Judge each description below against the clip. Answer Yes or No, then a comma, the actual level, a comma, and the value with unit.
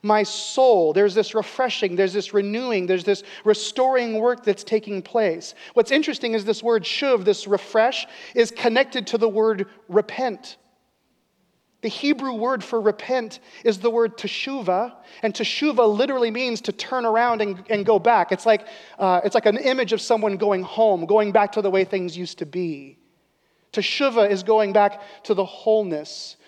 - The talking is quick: No, average, 170 wpm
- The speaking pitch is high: Yes, high, 220 Hz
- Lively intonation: No, average, 2.8 semitones